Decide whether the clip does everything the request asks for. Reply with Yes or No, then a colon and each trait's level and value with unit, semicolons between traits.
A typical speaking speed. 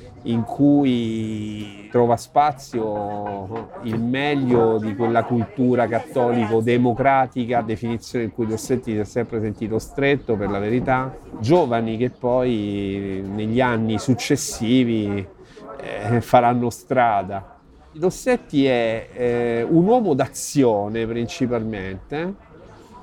No: slow, 100 wpm